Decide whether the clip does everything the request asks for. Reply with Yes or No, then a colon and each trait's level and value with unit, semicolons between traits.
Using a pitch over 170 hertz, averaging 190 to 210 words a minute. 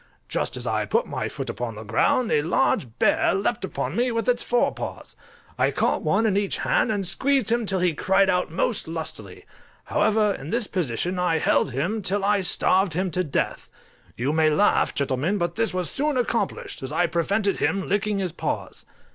Yes: high, 190 Hz; average, 195 wpm